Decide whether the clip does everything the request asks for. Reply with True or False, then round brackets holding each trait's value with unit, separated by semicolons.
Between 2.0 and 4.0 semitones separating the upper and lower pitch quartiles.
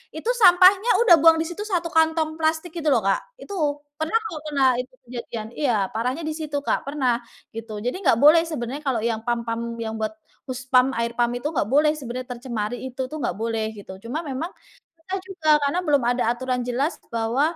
False (5.0 semitones)